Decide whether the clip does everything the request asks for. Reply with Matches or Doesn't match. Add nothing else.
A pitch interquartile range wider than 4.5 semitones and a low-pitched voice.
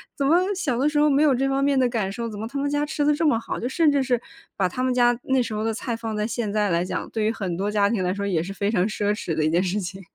Doesn't match